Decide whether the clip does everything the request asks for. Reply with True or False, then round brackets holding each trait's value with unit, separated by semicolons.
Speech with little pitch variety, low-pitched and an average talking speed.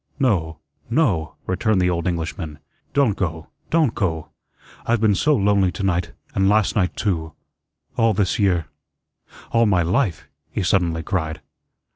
False (4.3 semitones; 95 Hz; 145 wpm)